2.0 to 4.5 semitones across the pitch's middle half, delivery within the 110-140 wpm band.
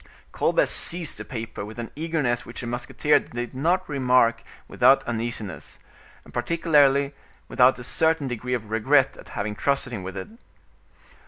No: average, 3.9 semitones; average, 155 wpm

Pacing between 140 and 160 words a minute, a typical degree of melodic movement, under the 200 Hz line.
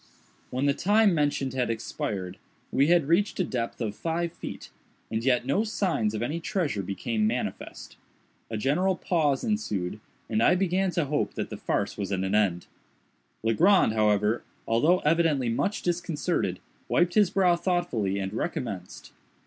No: average, 155 wpm; wide, 8.4 semitones; medium, 140 Hz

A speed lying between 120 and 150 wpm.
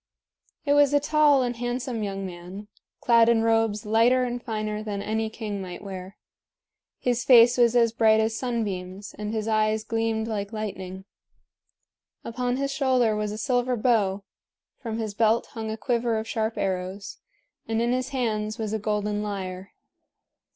No: average, 165 wpm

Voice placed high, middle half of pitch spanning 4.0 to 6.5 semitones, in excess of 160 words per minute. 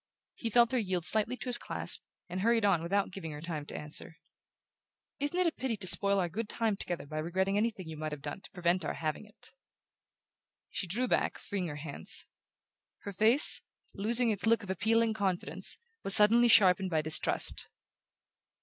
Yes: high, 195 Hz; average, 4.9 semitones; average, 185 wpm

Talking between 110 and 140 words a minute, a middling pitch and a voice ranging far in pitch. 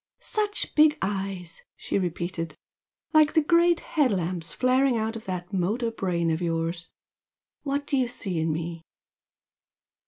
No: slow, 135 wpm; high, 195 Hz; wide, 8.1 semitones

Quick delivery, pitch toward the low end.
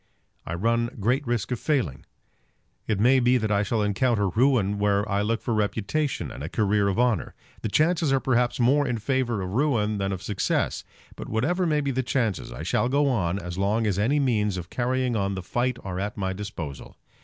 Yes: fast, 210 wpm; low, 110 Hz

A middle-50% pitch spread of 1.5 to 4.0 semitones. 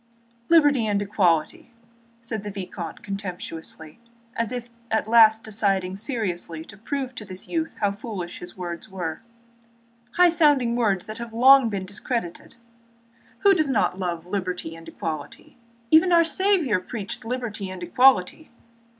No: wide, 5.4 semitones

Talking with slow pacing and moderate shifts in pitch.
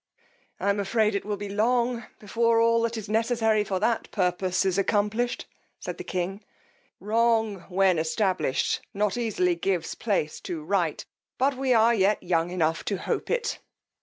No: average, 165 wpm; average, 3.7 semitones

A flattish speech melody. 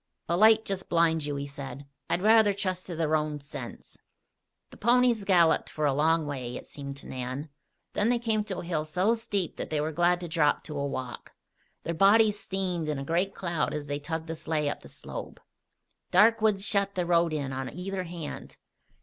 No: average, 4.8 semitones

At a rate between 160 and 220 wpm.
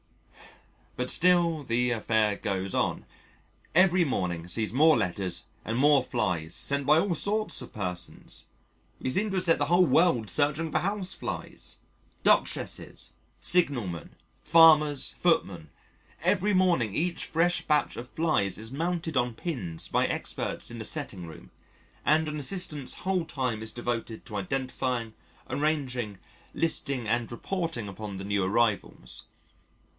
No: average, 140 wpm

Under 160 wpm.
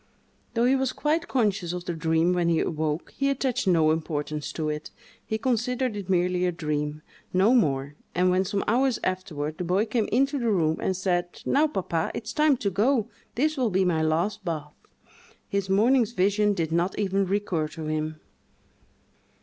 No: average, 175 wpm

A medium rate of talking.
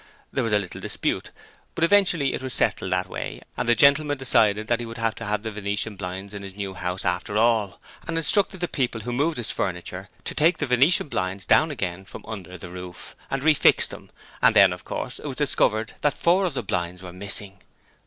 No: fast, 215 wpm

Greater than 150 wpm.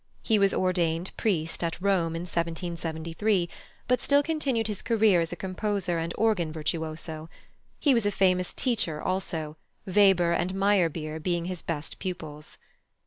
No: average, 145 wpm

